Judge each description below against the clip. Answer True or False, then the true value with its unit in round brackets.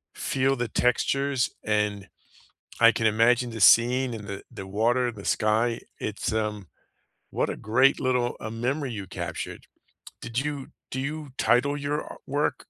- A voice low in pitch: True (120 Hz)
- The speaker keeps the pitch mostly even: False (3.6 semitones)